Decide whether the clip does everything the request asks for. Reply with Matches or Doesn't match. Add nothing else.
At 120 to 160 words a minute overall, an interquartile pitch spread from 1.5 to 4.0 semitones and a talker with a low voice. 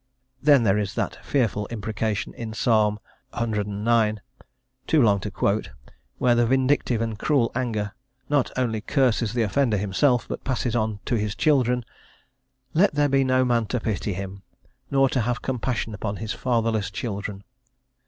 Matches